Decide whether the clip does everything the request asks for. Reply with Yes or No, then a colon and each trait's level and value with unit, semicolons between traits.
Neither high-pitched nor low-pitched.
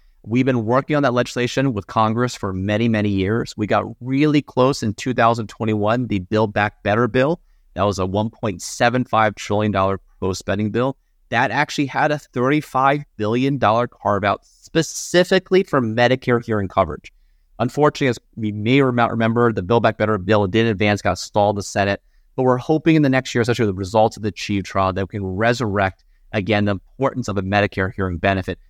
No: low, 110 Hz